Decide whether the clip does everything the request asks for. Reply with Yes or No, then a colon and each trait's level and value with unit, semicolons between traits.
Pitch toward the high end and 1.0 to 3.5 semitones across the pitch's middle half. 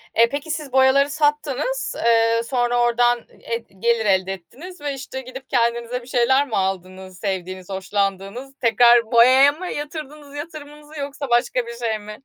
No: high, 245 Hz; average, 4.1 semitones